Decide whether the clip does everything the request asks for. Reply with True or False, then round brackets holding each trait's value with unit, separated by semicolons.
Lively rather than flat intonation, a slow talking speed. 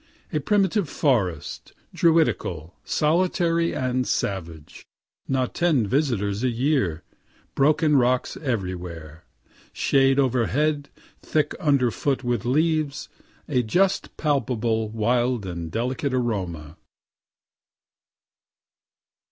True (6.1 semitones; 85 wpm)